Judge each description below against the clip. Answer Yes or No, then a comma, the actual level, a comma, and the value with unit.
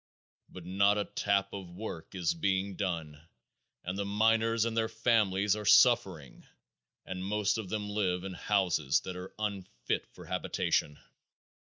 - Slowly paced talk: No, average, 150 wpm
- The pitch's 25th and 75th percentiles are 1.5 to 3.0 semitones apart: Yes, average, 2.7 semitones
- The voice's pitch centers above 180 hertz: No, low, 100 Hz